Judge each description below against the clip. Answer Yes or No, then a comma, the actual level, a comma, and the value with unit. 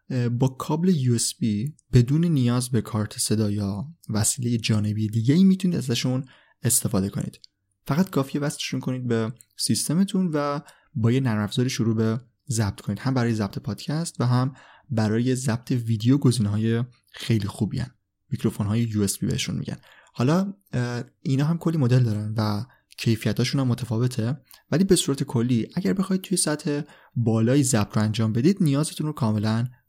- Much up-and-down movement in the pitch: No, average, 4.5 semitones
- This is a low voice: Yes, low, 120 Hz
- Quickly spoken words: Yes, fast, 160 wpm